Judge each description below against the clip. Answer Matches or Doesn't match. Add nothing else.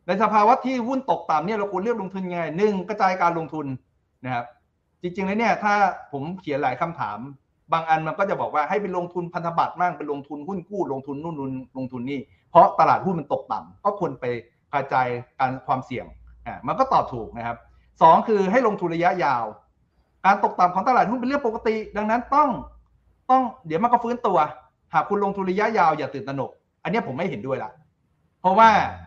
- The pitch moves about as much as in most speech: Doesn't match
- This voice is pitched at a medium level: Matches